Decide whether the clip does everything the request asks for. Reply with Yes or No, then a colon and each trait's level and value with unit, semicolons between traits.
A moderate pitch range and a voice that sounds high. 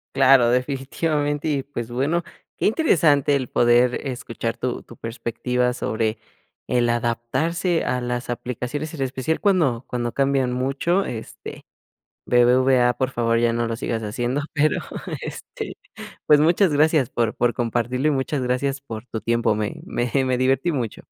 No: average, 3.2 semitones; low, 125 Hz